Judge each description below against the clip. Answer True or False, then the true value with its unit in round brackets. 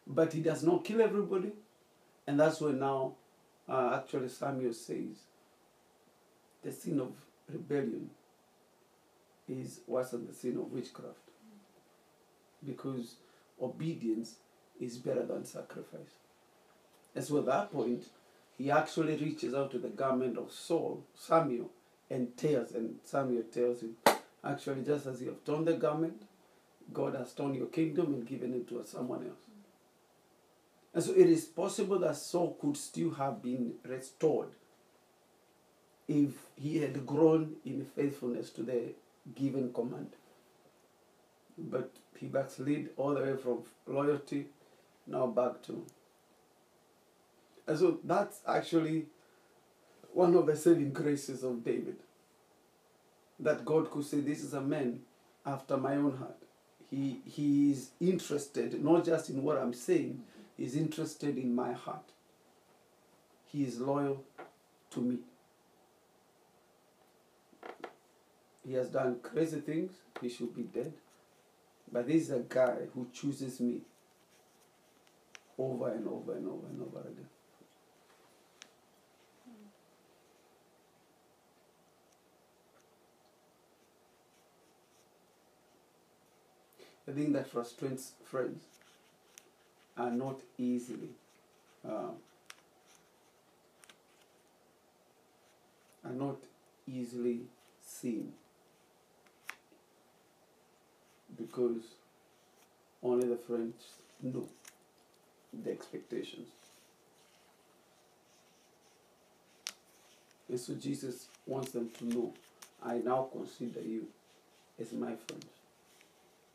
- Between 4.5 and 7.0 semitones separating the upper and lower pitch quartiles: False (3.7 semitones)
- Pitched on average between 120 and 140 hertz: True (135 Hz)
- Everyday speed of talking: False (105 wpm)